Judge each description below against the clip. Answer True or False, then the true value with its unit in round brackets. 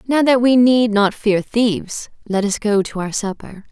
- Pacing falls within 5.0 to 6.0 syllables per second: False (4.4 syllables/s)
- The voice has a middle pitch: False (220 Hz)